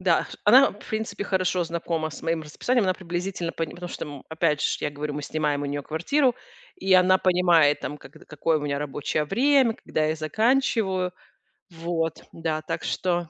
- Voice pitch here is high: No, medium, 170 Hz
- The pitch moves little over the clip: No, average, 3.5 semitones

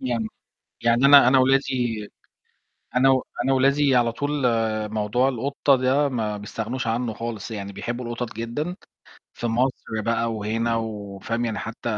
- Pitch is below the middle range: Yes, low, 120 Hz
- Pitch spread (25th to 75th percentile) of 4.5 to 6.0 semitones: No, average, 2.7 semitones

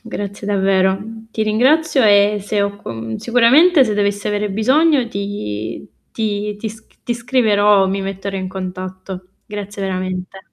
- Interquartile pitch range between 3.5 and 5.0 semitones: No, narrow, 2.5 semitones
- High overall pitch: Yes, high, 205 Hz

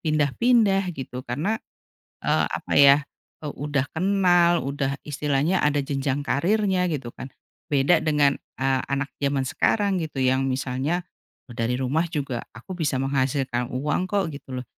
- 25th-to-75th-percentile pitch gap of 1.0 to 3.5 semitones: No, average, 4.5 semitones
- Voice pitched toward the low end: No, medium, 145 Hz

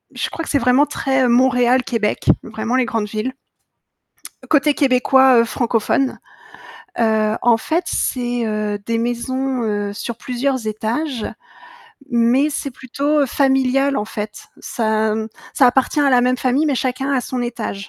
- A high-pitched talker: Yes, very high, 250 Hz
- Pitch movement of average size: Yes, average, 3.0 semitones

